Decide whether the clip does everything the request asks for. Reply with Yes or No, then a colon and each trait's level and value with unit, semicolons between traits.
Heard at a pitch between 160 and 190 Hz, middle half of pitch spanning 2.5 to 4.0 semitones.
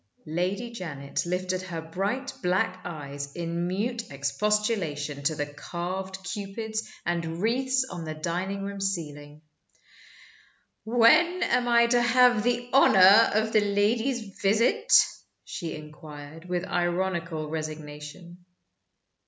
No: medium, 185 Hz; wide, 5.4 semitones